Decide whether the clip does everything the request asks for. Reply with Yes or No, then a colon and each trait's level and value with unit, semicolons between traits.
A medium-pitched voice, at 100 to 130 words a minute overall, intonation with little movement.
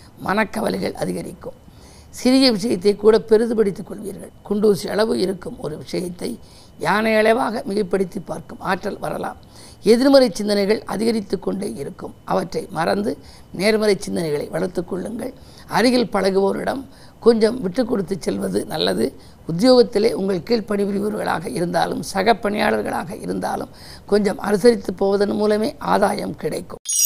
No: high, 210 Hz; average, 105 wpm; narrow, 2.2 semitones